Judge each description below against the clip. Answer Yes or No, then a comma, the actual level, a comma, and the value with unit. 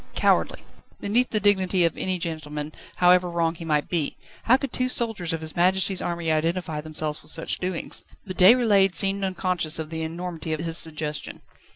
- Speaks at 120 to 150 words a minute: No, average, 180 wpm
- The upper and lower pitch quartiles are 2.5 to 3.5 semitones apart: Yes, average, 3.1 semitones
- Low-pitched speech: No, medium, 175 Hz